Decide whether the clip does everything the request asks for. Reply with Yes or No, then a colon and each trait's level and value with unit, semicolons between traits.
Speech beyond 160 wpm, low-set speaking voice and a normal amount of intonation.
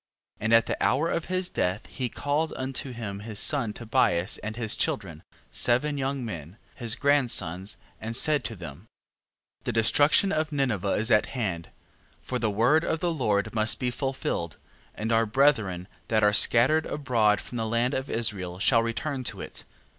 Yes: average, 180 wpm; low, 115 Hz; average, 4.6 semitones